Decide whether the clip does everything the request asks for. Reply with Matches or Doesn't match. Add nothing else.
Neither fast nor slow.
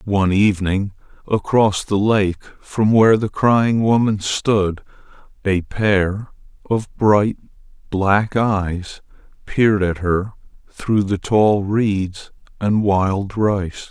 Doesn't match